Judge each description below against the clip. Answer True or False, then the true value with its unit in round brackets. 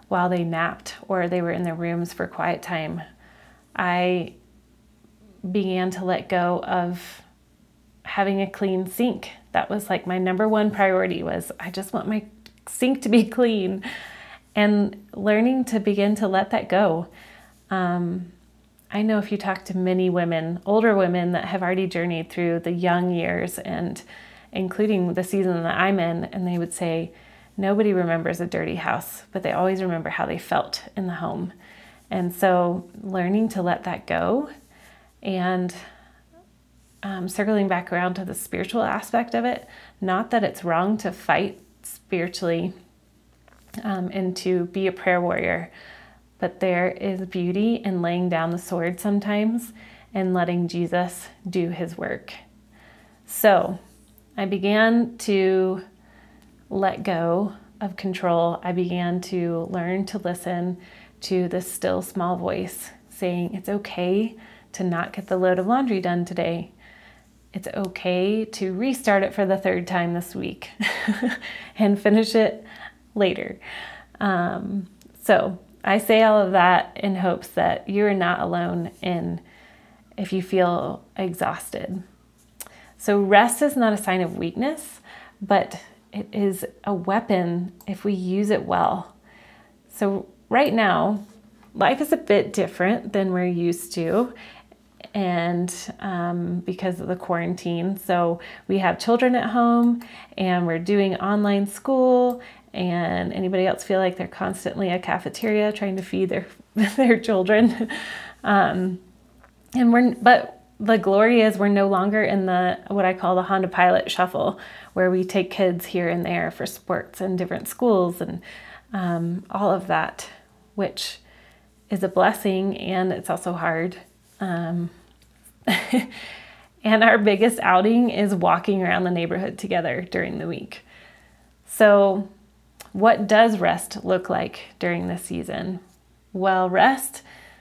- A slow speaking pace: False (145 wpm)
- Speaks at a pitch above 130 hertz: True (190 Hz)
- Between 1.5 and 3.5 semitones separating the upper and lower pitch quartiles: True (2.7 semitones)